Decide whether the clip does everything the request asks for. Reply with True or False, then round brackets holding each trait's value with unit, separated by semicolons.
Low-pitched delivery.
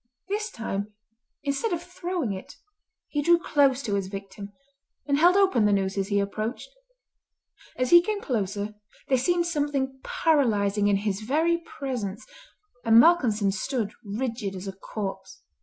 False (230 Hz)